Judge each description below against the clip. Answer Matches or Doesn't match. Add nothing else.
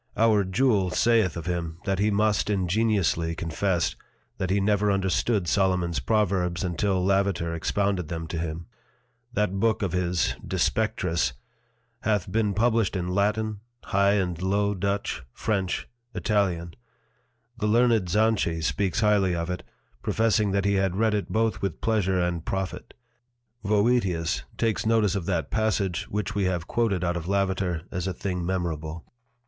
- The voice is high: Doesn't match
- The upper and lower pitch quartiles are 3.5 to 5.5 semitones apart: Doesn't match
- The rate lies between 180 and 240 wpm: Doesn't match